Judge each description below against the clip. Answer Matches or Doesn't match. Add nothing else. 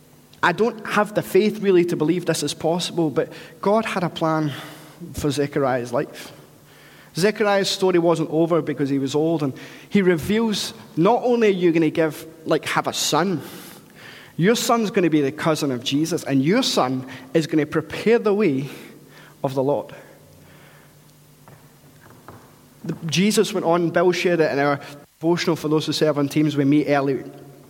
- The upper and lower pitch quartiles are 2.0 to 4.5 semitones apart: Matches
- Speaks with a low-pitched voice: Doesn't match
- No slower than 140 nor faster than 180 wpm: Matches